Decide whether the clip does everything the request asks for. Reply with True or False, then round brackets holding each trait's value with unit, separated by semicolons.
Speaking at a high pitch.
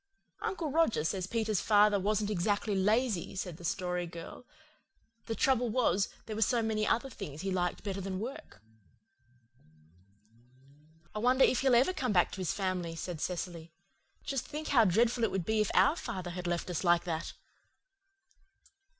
True (205 Hz)